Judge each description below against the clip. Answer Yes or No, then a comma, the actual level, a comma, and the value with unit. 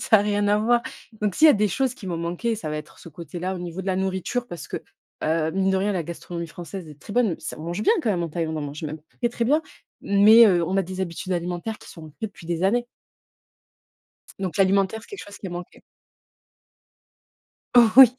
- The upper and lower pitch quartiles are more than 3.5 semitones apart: Yes, average, 3.9 semitones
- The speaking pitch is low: No, high, 190 Hz